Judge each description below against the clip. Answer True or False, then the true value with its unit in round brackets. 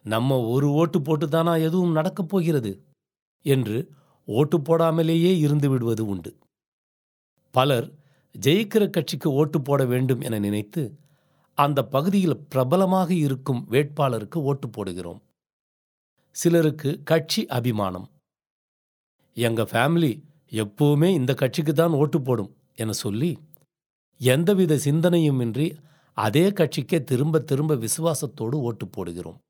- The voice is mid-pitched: True (145 Hz)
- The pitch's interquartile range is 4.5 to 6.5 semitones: True (4.8 semitones)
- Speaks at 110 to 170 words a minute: False (100 wpm)